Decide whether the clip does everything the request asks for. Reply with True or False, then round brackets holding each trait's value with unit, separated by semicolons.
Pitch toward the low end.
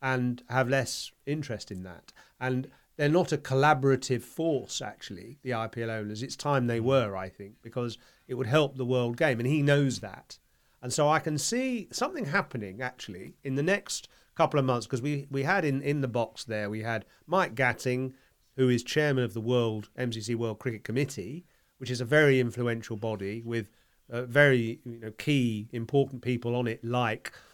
True (125 Hz)